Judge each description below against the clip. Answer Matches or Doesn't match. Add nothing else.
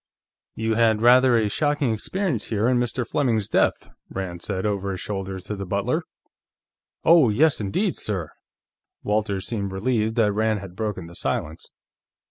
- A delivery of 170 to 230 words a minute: Doesn't match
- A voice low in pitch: Matches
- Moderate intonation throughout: Matches